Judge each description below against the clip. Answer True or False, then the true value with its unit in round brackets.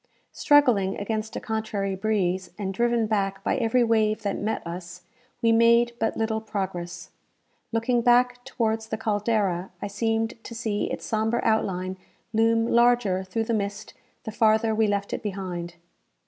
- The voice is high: True (220 Hz)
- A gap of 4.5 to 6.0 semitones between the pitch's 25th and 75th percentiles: False (2.6 semitones)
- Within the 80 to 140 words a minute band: False (155 wpm)